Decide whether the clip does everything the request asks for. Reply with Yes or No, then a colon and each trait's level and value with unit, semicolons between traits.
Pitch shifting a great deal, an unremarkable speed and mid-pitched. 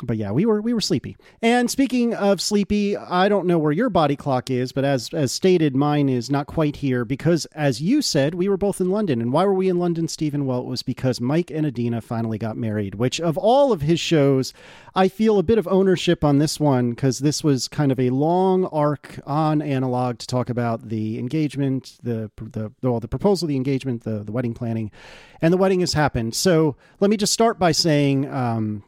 No: wide, 6.1 semitones; fast, 225 wpm; medium, 145 Hz